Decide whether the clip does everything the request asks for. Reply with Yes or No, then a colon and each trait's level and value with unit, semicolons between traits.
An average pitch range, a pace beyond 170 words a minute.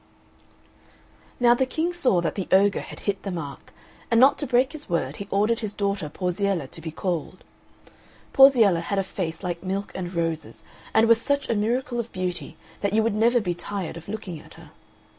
Yes: average, 4.8 semitones; average, 200 wpm